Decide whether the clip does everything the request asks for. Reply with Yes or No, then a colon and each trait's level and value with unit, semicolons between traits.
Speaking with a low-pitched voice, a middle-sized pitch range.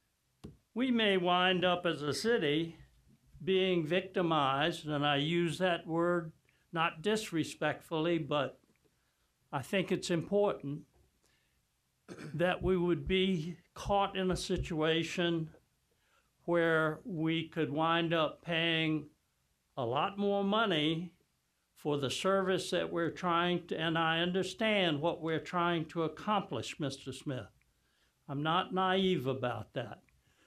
No: medium, 165 Hz; average, 3.4 semitones